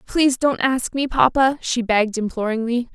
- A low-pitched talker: No, high, 245 Hz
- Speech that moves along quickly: No, average, 165 wpm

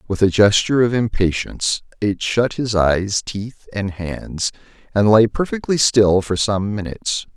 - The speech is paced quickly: No, average, 155 wpm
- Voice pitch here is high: No, low, 105 Hz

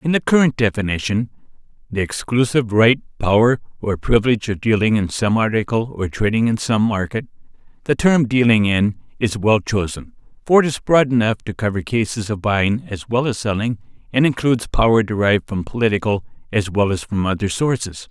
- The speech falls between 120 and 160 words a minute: No, average, 175 wpm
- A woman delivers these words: No, male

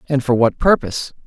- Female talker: No, male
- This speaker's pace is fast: No, average, 190 wpm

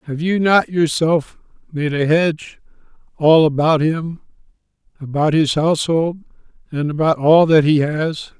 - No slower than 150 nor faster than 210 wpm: No, slow, 135 wpm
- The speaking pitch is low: No, medium, 155 Hz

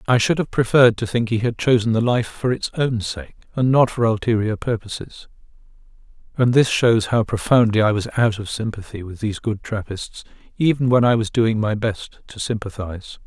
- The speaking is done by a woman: No, male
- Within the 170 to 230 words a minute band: Yes, average, 195 wpm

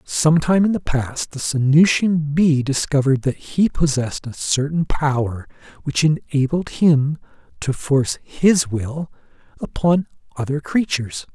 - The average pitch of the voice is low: No, medium, 145 Hz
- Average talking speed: No, slow, 130 wpm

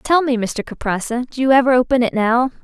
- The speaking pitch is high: Yes, very high, 250 Hz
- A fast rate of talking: Yes, fast, 230 wpm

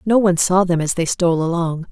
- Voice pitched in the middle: Yes, medium, 175 Hz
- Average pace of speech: No, fast, 250 wpm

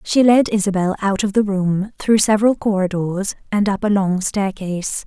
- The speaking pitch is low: No, high, 200 Hz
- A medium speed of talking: Yes, average, 180 wpm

